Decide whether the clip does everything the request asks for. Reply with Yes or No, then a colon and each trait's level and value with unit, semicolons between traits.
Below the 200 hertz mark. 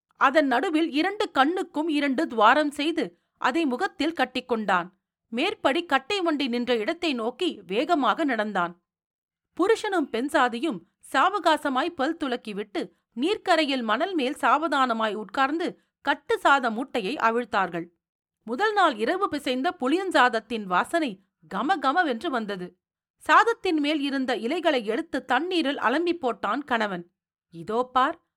No: very high, 275 Hz